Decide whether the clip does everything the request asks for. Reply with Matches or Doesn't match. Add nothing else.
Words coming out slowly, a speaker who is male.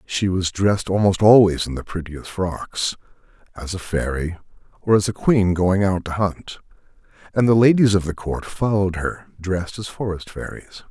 Doesn't match